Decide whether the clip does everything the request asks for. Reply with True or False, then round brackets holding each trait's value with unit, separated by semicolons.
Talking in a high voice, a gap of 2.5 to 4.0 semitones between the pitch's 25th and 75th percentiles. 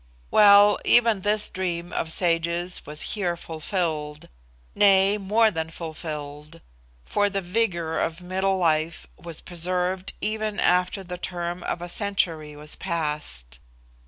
False (175 Hz; 3.3 semitones)